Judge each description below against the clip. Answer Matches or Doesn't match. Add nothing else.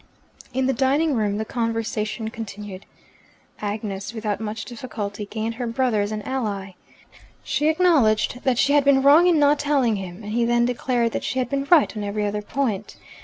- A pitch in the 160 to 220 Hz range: Doesn't match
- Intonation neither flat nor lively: Matches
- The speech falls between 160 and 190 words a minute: Matches